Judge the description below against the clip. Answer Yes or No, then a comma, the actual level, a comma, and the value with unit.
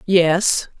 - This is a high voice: No, medium, 180 Hz